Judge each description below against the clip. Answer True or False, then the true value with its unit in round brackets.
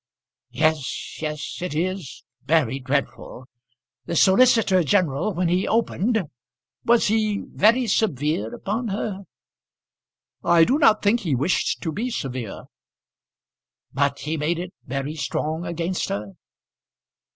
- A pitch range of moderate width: False (6.0 semitones)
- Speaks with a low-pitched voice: False (170 Hz)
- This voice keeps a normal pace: False (120 wpm)